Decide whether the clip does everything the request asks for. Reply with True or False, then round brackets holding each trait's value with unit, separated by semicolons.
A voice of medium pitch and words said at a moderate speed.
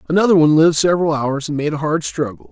False (155 Hz; 240 wpm)